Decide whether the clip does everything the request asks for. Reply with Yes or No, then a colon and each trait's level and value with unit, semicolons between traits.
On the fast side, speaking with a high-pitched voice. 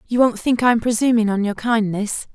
Yes: fast, 230 wpm; high, 225 Hz